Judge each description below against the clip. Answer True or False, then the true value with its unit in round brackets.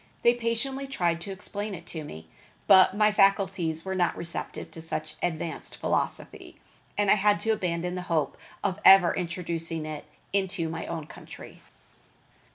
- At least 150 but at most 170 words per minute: True (160 wpm)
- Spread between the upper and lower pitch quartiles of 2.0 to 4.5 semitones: True (3.4 semitones)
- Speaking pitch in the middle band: True (180 Hz)